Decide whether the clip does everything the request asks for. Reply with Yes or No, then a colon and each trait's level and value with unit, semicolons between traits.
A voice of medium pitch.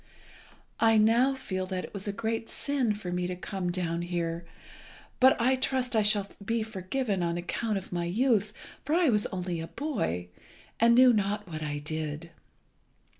No: high, 200 Hz